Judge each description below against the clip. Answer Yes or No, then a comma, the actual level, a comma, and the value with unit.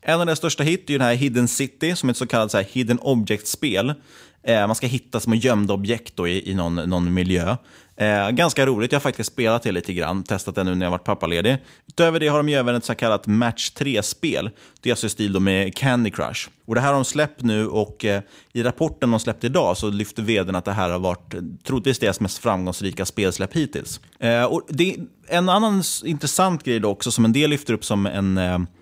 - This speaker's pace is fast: Yes, fast, 235 wpm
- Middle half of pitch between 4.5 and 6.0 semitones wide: Yes, wide, 5.4 semitones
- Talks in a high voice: No, low, 115 Hz